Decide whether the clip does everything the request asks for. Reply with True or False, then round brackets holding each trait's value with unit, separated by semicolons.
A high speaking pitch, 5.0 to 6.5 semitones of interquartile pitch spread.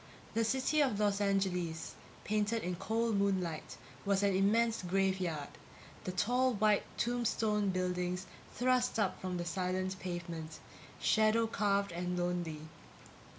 False (195 Hz; 3.3 semitones)